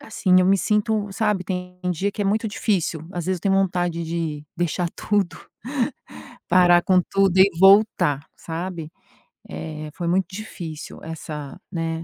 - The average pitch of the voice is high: No, medium, 180 Hz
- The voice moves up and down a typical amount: Yes, average, 3.0 semitones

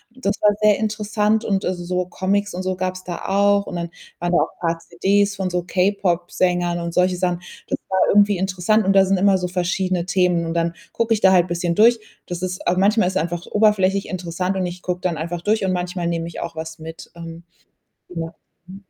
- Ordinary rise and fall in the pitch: No, narrow, 2.3 semitones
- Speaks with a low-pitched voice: No, medium, 185 Hz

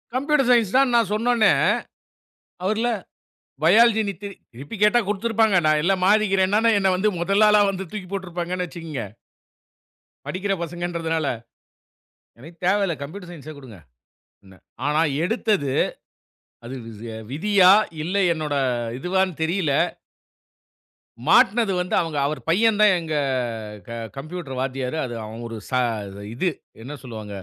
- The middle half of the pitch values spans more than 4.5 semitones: Yes, wide, 5.5 semitones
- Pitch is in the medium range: Yes, medium, 180 Hz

